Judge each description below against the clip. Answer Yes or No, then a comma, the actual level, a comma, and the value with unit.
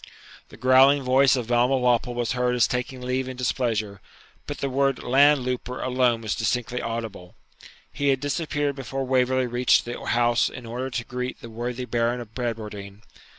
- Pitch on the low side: Yes, low, 125 Hz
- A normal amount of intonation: No, narrow, 1.6 semitones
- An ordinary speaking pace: Yes, average, 170 wpm